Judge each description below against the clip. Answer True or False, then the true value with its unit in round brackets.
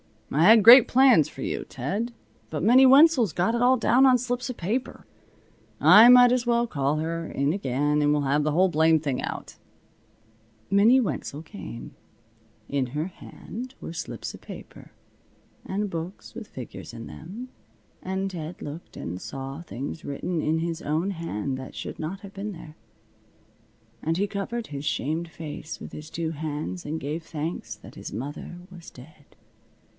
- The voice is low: False (165 Hz)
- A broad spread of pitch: True (6.6 semitones)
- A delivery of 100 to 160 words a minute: False (170 wpm)